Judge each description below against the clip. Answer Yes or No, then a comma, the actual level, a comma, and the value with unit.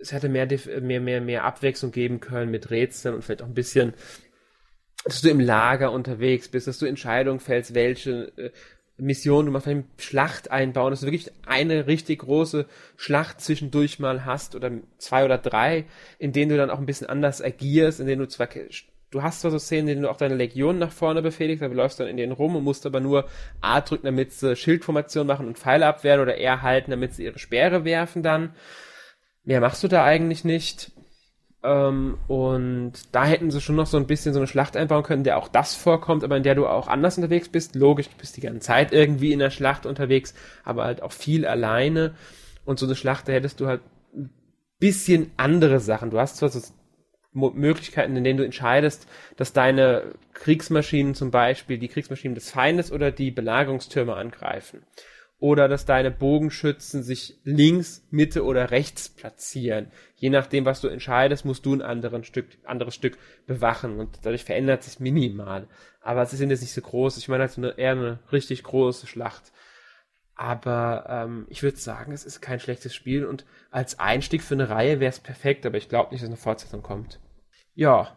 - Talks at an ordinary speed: No, fast, 195 wpm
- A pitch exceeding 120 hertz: Yes, low, 135 Hz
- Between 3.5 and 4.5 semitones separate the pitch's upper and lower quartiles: No, average, 2.7 semitones